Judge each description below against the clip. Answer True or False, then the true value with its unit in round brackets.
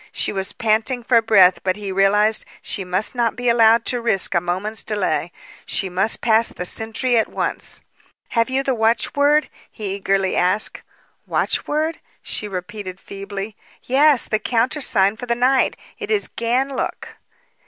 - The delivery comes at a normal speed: True (155 wpm)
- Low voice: False (220 Hz)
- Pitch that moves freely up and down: False (3.9 semitones)